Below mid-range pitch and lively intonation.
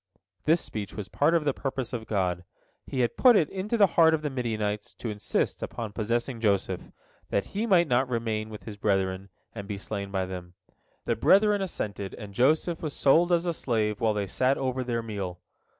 Yes: low, 115 Hz; wide, 6.8 semitones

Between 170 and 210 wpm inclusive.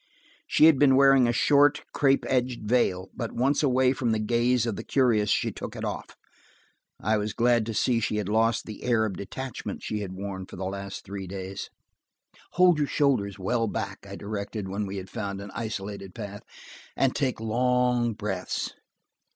Yes: average, 185 wpm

